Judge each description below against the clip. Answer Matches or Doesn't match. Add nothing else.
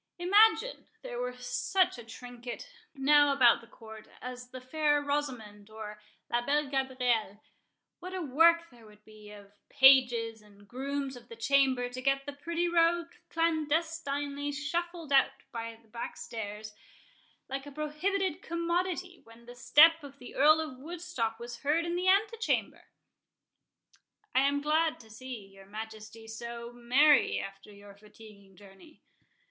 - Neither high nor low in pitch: Doesn't match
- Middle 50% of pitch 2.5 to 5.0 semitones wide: Doesn't match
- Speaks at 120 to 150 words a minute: Matches